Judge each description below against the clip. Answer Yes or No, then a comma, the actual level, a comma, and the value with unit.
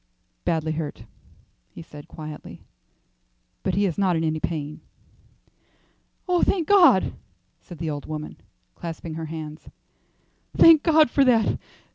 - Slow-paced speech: Yes, slow, 130 wpm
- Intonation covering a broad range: Yes, wide, 6.6 semitones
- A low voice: No, medium, 165 Hz